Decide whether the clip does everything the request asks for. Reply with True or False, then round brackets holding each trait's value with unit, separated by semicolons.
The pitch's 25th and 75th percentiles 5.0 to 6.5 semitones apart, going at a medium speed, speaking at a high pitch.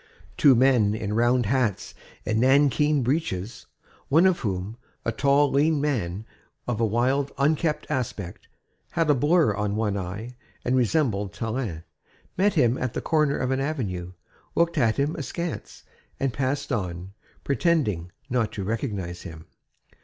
False (5.5 semitones; 145 wpm; 125 Hz)